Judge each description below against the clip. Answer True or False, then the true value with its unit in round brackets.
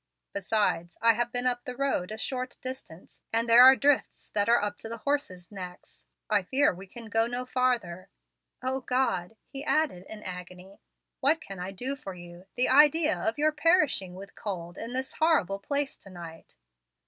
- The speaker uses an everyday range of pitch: False (6.1 semitones)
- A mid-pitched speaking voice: False (230 Hz)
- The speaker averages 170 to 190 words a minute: True (185 wpm)